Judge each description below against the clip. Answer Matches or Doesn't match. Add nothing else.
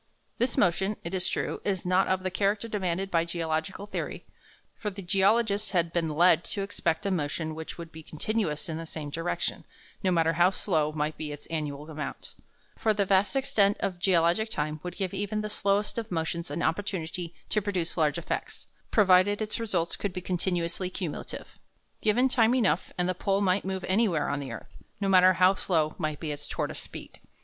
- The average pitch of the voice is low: Doesn't match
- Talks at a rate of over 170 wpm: Matches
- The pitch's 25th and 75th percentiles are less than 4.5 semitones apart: Matches